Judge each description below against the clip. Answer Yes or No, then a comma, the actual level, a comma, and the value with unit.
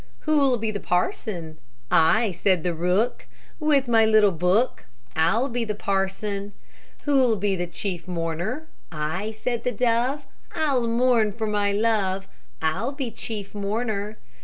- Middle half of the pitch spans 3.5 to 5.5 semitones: Yes, average, 4.0 semitones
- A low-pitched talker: No, high, 215 Hz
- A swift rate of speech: No, slow, 135 wpm